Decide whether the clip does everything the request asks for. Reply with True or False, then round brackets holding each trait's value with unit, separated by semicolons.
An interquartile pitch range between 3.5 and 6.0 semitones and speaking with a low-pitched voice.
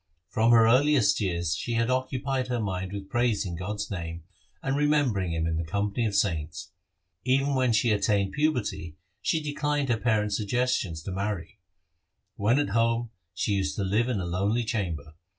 True (4.8 semitones; 105 Hz)